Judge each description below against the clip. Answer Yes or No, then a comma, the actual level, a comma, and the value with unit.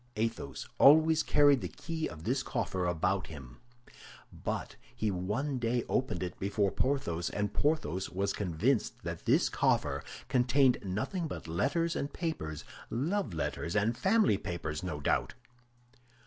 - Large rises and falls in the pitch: Yes, wide, 7.9 semitones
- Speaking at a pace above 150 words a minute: No, slow, 135 wpm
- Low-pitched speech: Yes, low, 110 Hz